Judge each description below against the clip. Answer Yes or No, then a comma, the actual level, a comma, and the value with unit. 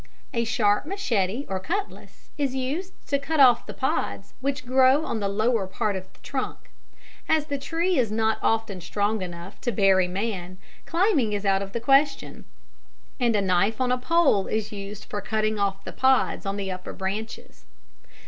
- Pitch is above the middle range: Yes, high, 220 Hz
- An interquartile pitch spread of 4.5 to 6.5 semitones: Yes, average, 5.2 semitones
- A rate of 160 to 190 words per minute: Yes, average, 185 wpm